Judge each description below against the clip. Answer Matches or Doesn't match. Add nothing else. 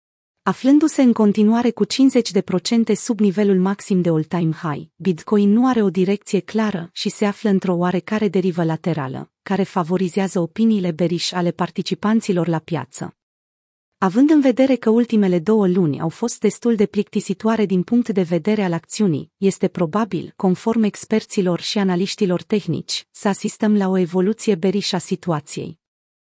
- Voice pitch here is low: Doesn't match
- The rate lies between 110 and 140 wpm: Doesn't match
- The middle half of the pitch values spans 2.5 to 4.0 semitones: Matches